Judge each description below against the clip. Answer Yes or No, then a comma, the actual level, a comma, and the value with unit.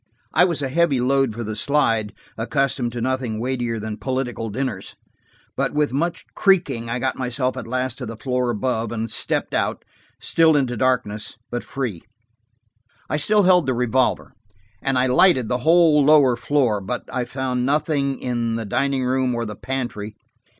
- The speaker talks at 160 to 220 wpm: Yes, average, 170 wpm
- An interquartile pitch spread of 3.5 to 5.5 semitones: No, average, 2.8 semitones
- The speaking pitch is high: No, low, 130 Hz